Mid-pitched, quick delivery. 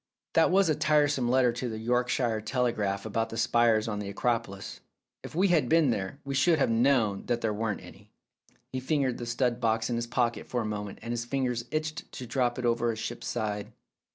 No: low, 120 Hz; fast, 210 wpm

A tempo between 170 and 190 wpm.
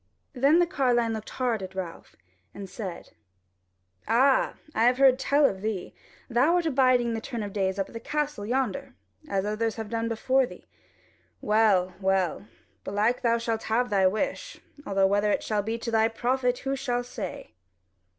Yes: average, 180 wpm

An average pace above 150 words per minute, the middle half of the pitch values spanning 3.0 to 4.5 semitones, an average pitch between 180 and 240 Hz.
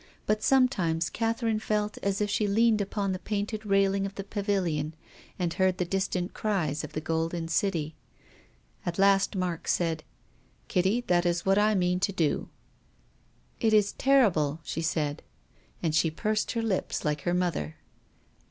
Yes: average, 170 wpm; average, 4.0 semitones; high, 190 Hz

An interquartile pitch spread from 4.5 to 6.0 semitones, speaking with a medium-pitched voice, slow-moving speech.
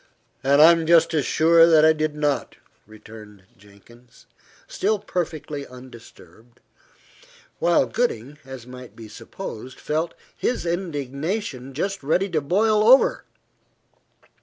Yes: average, 5.3 semitones; medium, 150 Hz; slow, 120 wpm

